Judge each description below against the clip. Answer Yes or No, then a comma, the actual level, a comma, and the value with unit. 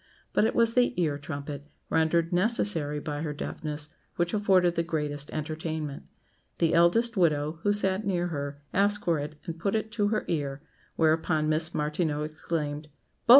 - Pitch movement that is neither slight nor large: Yes, average, 3.9 semitones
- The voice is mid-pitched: Yes, medium, 160 Hz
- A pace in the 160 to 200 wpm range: Yes, average, 165 wpm